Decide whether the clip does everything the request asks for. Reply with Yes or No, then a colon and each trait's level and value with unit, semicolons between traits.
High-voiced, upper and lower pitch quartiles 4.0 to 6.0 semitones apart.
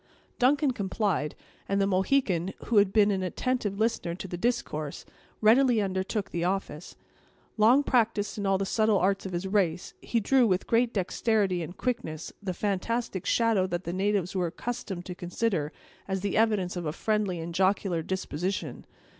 No: high, 195 Hz; average, 3.5 semitones